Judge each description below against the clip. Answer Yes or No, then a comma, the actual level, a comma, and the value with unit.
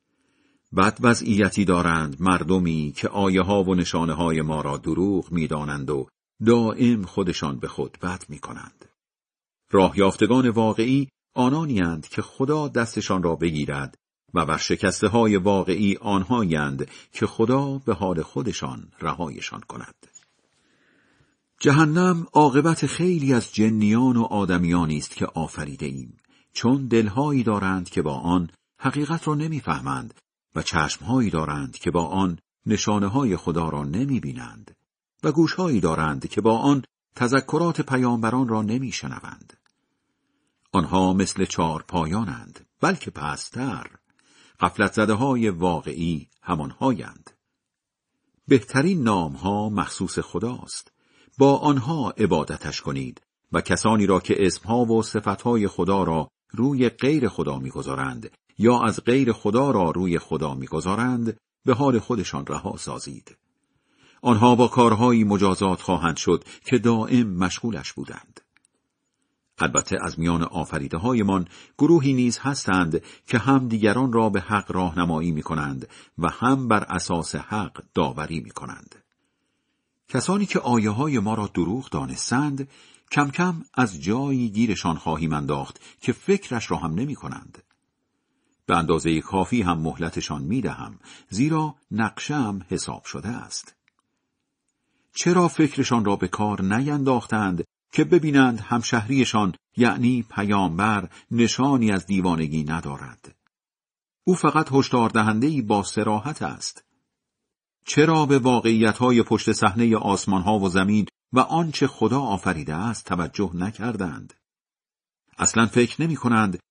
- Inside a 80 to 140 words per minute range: Yes, average, 125 wpm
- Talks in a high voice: No, low, 105 Hz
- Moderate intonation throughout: No, wide, 6.3 semitones